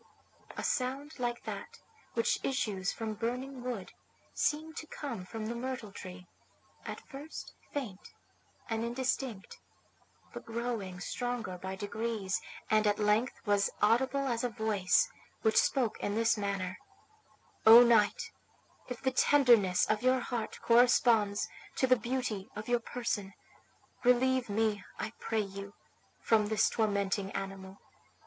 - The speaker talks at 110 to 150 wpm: Yes, slow, 135 wpm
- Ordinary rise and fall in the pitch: Yes, average, 3.5 semitones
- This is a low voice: No, high, 225 Hz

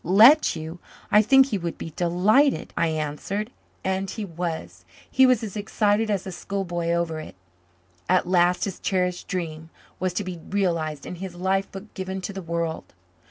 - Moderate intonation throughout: Yes, average, 3.2 semitones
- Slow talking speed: No, average, 175 wpm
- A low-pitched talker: No, medium, 185 Hz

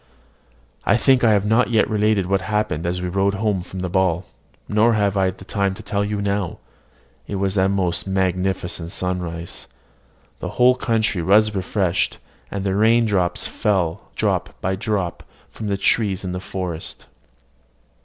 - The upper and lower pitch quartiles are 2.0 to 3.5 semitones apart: Yes, narrow, 2.4 semitones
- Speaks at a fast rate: No, average, 160 wpm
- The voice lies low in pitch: Yes, very low, 95 Hz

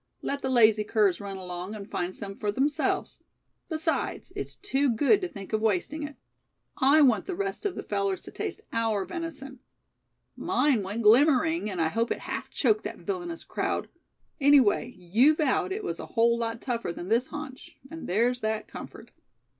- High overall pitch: Yes, high, 240 Hz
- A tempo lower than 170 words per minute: No, average, 180 wpm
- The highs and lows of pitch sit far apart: Yes, wide, 6.3 semitones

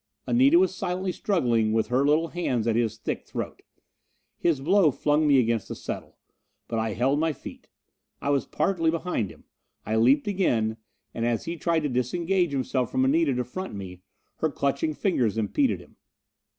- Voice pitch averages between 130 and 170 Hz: Yes, medium, 140 Hz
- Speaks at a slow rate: No, average, 175 wpm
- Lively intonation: Yes, wide, 6.3 semitones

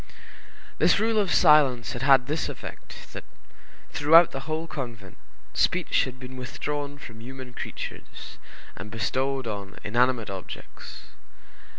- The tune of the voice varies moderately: Yes, average, 3.8 semitones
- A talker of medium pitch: No, low, 130 Hz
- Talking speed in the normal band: No, slow, 125 wpm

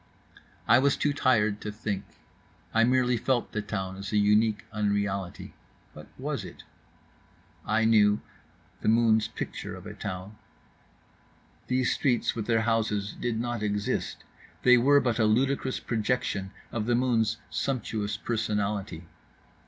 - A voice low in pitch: Yes, low, 110 Hz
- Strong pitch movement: No, average, 2.7 semitones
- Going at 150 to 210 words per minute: No, slow, 135 wpm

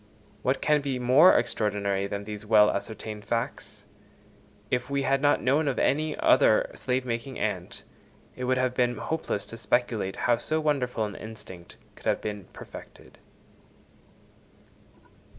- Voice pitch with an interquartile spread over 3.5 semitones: Yes, average, 4.4 semitones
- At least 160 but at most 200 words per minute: No, average, 145 wpm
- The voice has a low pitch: Yes, low, 125 Hz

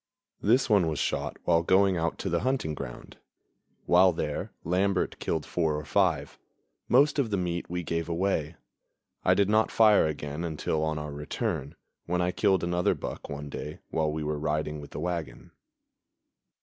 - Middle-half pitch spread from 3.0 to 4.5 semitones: Yes, average, 3.9 semitones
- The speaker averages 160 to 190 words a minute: Yes, average, 175 wpm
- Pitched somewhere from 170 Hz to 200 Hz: No, very low, 85 Hz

